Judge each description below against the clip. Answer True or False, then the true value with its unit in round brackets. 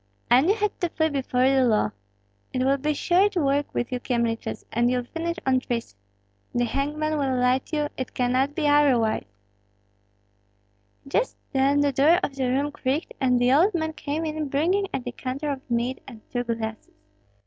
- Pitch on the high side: True (270 Hz)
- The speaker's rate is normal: True (180 wpm)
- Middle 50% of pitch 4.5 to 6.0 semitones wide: False (3.5 semitones)